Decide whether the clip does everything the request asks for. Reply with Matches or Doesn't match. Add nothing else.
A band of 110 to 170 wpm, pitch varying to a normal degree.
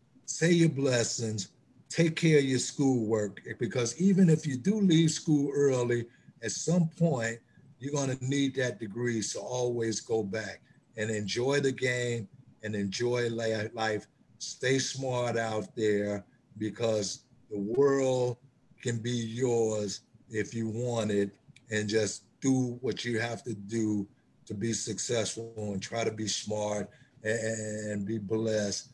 Matches